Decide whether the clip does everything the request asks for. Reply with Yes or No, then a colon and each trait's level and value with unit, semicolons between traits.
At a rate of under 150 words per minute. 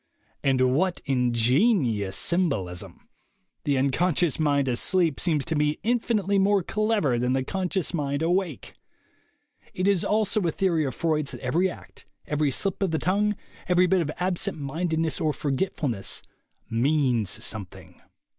Yes: average, 140 wpm